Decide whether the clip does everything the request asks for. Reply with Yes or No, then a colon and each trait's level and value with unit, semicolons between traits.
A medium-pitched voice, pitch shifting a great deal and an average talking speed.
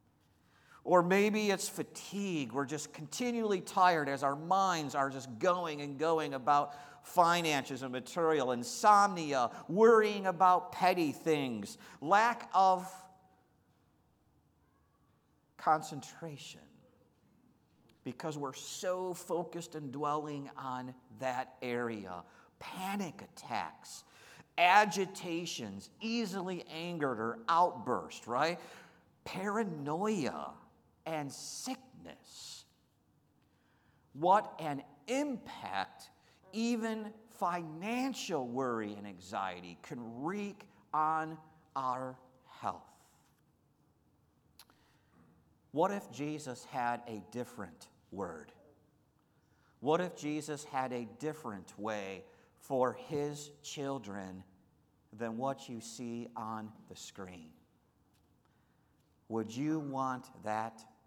No: medium, 150 Hz; wide, 6.4 semitones; slow, 85 wpm